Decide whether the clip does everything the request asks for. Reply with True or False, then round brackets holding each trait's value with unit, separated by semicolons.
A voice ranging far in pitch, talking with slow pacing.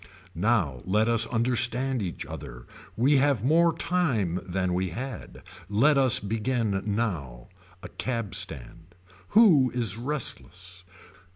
True (6.0 semitones; 120 wpm)